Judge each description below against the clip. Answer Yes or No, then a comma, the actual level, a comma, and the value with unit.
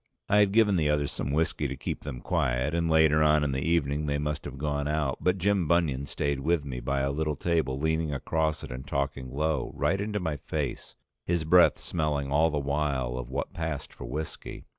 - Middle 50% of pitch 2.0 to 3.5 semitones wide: Yes, average, 2.7 semitones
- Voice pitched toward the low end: Yes, very low, 75 Hz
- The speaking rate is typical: No, fast, 215 wpm